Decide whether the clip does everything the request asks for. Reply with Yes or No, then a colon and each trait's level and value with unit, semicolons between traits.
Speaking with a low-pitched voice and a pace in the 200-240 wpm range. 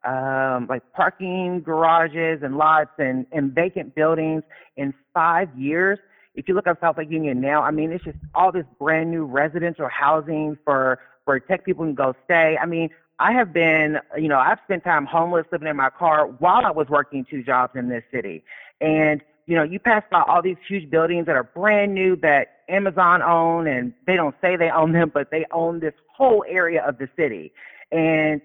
No: medium, 160 Hz; fast, 205 wpm